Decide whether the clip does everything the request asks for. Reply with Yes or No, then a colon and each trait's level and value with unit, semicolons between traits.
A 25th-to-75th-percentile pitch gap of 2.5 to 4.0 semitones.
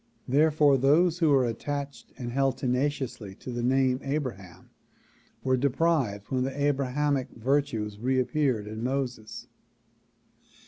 Yes: average, 2.8 semitones